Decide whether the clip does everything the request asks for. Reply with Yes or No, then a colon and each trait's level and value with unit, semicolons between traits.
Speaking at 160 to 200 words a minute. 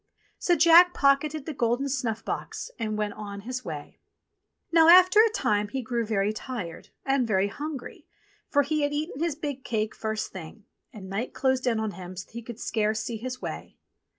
Yes: average, 195 wpm